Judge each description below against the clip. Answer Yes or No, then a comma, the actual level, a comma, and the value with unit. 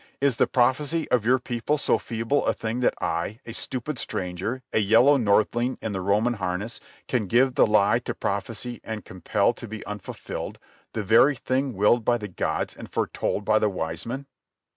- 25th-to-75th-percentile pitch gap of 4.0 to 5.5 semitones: No, average, 3.5 semitones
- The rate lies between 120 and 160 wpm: No, average, 185 wpm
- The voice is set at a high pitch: No, low, 115 Hz